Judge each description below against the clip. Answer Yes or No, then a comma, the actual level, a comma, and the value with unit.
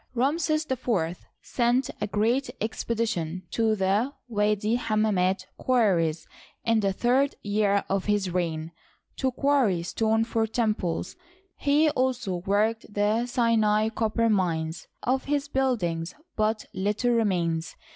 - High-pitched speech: Yes, high, 215 Hz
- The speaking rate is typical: No, slow, 125 wpm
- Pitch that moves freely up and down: No, average, 4.1 semitones